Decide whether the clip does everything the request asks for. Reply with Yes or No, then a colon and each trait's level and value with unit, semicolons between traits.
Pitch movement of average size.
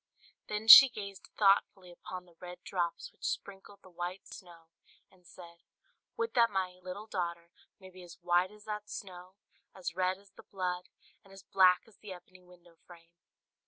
No: narrow, 2.0 semitones